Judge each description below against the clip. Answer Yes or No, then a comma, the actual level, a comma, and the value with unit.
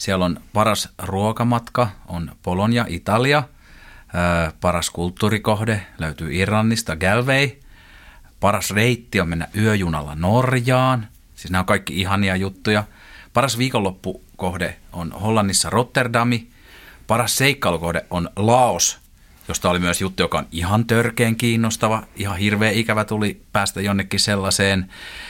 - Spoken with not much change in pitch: No, average, 3.9 semitones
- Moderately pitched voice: No, low, 100 Hz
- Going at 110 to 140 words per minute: Yes, average, 120 wpm